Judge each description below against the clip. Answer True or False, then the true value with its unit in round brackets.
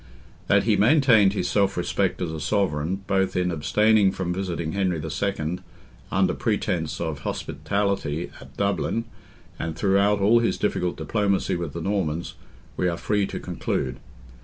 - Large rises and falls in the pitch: False (3.4 semitones)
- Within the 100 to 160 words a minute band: True (150 wpm)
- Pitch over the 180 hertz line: False (95 Hz)